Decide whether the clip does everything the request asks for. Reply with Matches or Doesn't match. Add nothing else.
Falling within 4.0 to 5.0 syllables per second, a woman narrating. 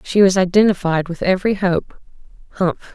Doesn't match